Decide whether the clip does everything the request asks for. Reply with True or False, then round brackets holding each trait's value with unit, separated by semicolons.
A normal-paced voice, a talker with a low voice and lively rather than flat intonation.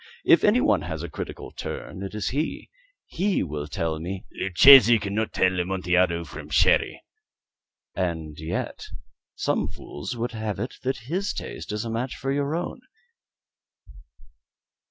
True (150 wpm; 100 Hz; 6.6 semitones)